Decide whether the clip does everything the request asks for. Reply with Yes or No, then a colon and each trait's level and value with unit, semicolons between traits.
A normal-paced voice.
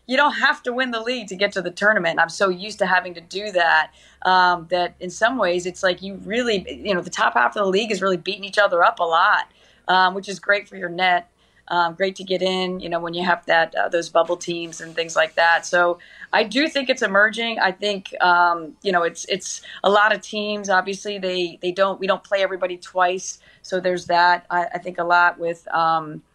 No: fast, 245 wpm